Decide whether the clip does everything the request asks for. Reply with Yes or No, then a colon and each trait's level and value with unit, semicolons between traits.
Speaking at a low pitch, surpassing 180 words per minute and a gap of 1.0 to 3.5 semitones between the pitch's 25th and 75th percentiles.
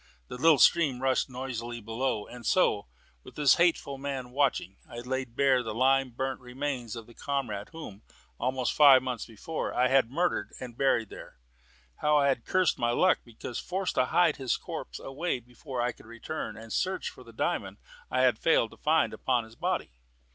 Yes: low, 130 Hz; average, 190 wpm; average, 2.9 semitones